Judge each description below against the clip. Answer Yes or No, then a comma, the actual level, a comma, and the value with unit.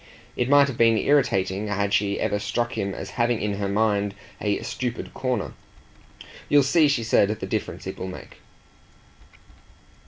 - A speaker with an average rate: Yes, average, 160 wpm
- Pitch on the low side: Yes, low, 110 Hz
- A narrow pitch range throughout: No, average, 3.5 semitones